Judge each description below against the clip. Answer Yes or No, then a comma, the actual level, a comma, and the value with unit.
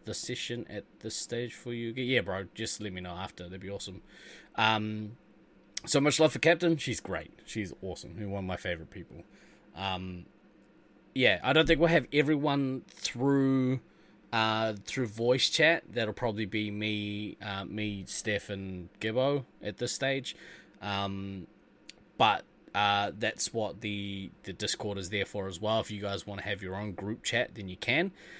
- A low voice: Yes, low, 105 Hz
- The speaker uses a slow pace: No, average, 175 wpm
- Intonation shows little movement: No, average, 3.8 semitones